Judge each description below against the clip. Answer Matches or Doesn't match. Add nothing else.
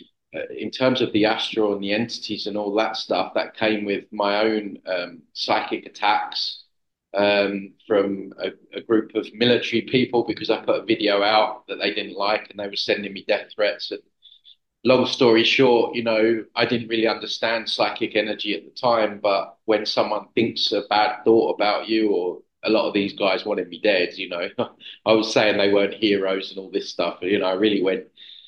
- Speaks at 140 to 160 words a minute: Doesn't match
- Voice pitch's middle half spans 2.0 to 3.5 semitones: Matches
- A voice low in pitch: Matches